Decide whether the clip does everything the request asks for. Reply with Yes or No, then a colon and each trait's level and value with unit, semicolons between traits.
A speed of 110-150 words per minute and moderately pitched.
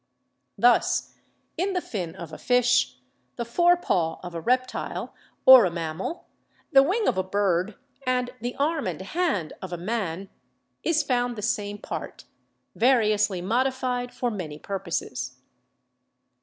No: average, 145 wpm; high, 215 Hz